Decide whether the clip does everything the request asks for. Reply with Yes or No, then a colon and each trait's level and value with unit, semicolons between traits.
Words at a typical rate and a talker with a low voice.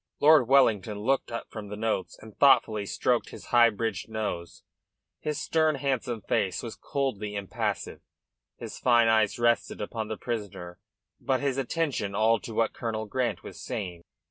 Yes: average, 160 wpm; low, 115 Hz